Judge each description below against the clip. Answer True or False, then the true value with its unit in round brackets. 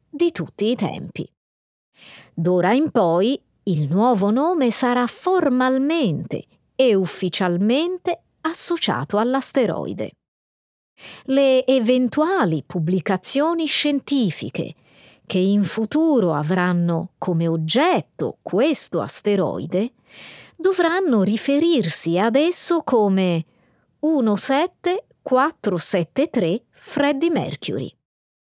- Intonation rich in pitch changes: True (7.9 semitones)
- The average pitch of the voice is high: True (240 Hz)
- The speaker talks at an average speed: False (75 wpm)